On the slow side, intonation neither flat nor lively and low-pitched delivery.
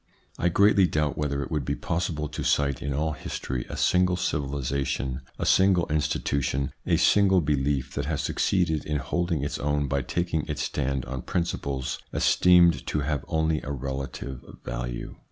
No: average, 165 wpm; average, 3.5 semitones; very low, 75 Hz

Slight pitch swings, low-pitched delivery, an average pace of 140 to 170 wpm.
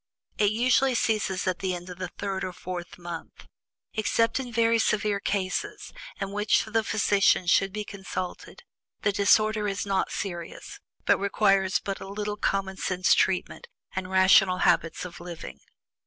No: narrow, 2.3 semitones; high, 195 Hz; average, 155 wpm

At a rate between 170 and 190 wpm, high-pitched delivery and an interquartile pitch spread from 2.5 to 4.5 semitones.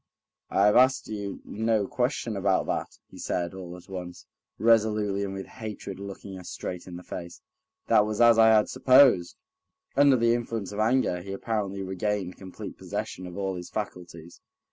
No: average, 175 wpm; low, 100 Hz; average, 3.3 semitones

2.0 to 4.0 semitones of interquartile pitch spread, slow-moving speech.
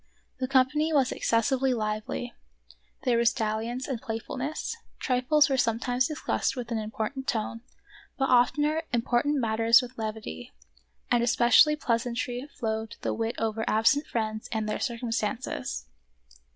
Yes: average, 2.9 semitones; slow, 130 wpm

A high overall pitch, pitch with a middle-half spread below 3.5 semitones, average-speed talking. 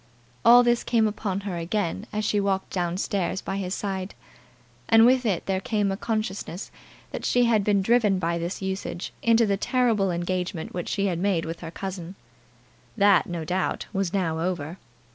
Yes: high, 195 Hz; average, 3.0 semitones; average, 180 wpm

